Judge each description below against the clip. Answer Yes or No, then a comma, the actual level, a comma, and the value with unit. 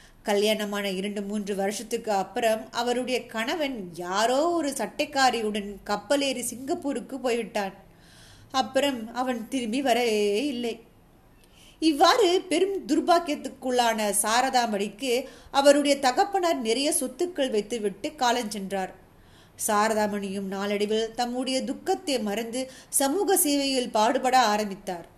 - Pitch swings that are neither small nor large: Yes, average, 4.7 semitones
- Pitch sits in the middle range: No, high, 240 Hz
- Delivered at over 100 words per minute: No, average, 90 wpm